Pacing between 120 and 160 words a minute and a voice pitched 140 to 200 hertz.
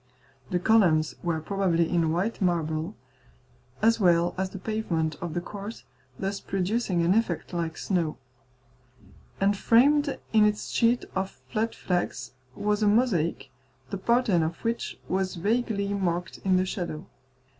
Yes: average, 145 wpm; high, 190 Hz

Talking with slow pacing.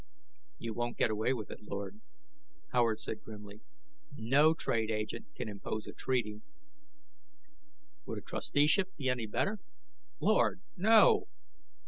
Yes: slow, 130 wpm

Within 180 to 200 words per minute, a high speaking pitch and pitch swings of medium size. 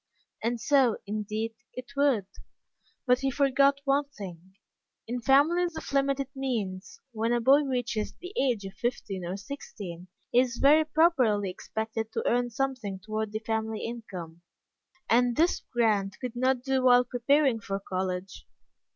No: average, 150 wpm; high, 240 Hz; average, 4.4 semitones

